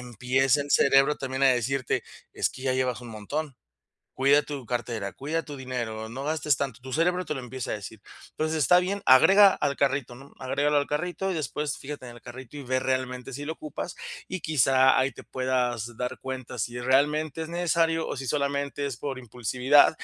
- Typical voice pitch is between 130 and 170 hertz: Yes, low, 135 Hz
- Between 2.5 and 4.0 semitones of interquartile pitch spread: Yes, average, 2.9 semitones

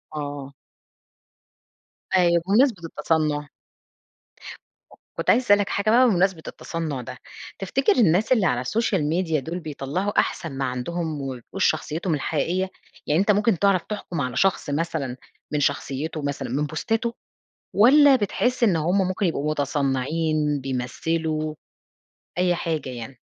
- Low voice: No, medium, 165 Hz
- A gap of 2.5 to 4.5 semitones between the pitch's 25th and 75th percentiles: No, average, 5.1 semitones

